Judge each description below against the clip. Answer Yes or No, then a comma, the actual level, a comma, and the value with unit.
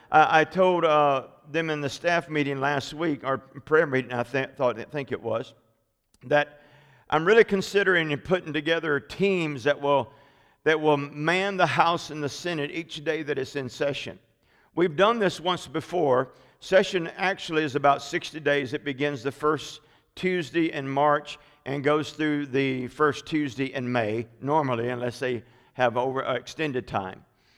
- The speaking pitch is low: No, medium, 145 Hz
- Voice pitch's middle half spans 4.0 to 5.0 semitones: No, average, 3.0 semitones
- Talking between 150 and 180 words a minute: Yes, average, 170 wpm